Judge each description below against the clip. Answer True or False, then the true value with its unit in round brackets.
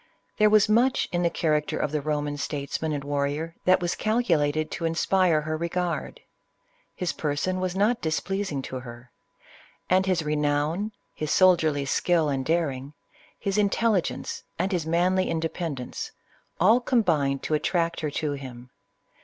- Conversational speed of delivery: True (150 wpm)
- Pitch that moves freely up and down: False (4.1 semitones)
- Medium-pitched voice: True (160 Hz)